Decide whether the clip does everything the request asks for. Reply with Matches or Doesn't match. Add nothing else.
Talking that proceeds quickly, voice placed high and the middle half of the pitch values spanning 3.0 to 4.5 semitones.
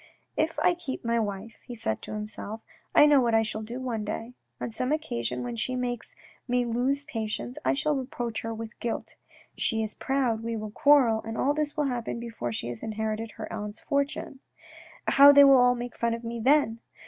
Matches